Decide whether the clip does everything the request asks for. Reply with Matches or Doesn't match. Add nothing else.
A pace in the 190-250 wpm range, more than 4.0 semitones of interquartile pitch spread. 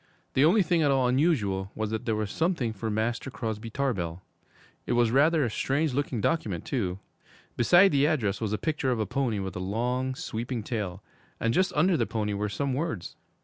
Matches